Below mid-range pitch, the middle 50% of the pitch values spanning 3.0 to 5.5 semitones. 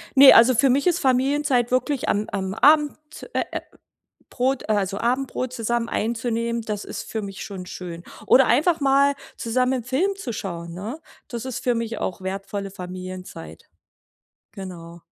No: high, 235 Hz; average, 5.2 semitones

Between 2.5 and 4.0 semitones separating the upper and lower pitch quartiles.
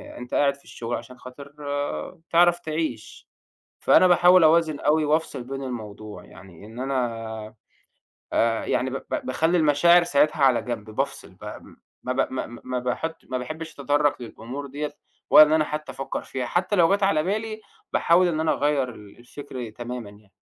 No: average, 4.7 semitones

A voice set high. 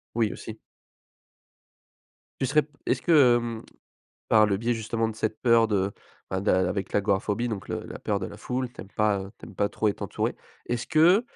No: low, 110 Hz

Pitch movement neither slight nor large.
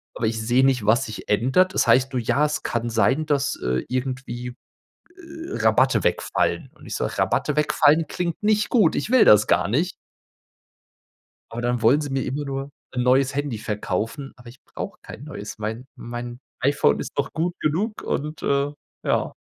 Yes: average, 4.2 semitones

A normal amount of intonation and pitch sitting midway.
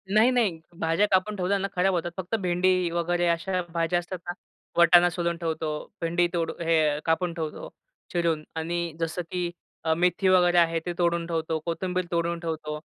No: narrow, 1.5 semitones; medium, 170 Hz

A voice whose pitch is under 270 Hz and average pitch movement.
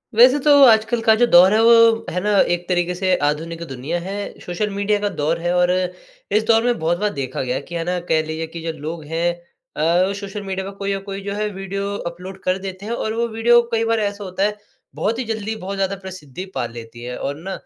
Yes: high, 190 Hz; average, 3.8 semitones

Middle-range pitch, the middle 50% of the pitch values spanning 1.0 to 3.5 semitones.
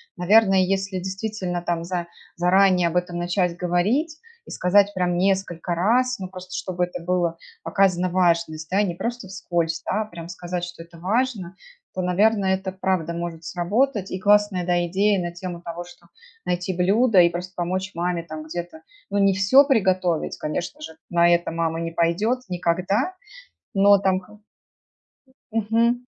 Yes: medium, 180 Hz; narrow, 2.4 semitones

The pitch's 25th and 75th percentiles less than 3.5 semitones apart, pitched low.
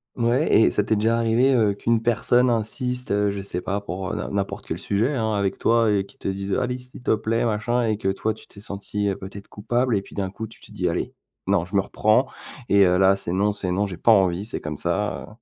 Yes: average, 2.9 semitones; low, 105 Hz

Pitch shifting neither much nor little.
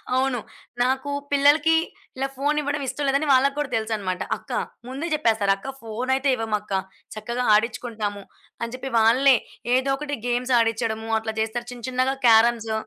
Yes: average, 3.4 semitones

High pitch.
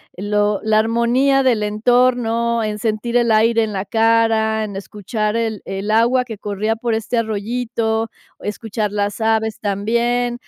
Yes: high, 220 Hz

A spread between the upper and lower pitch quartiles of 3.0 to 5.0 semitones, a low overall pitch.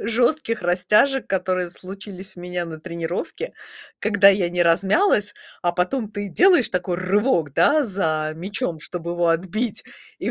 No: average, 3.7 semitones; medium, 185 Hz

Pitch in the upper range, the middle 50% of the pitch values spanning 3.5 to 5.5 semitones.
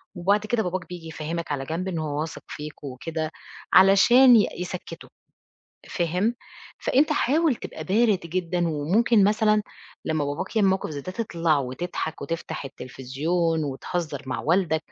No: medium, 170 Hz; average, 4.2 semitones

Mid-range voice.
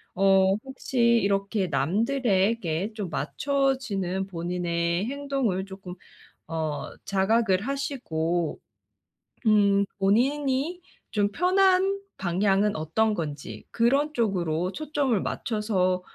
No: high, 200 Hz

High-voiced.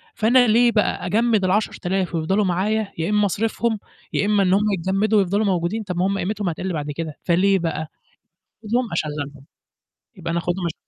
Yes: high, 195 Hz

